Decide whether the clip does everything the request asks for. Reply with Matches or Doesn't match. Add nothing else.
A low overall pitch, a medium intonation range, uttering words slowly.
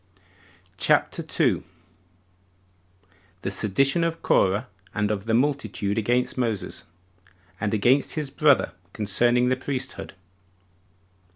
Matches